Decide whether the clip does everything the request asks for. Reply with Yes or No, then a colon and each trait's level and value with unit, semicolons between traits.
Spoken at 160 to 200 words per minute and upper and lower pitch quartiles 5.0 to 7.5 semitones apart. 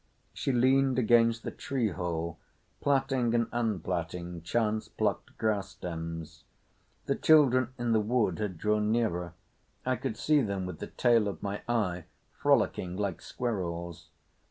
No: average, 140 wpm; average, 5.3 semitones